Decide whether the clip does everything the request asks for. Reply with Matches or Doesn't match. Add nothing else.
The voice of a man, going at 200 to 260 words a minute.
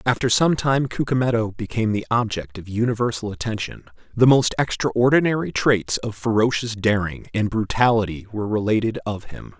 Doesn't match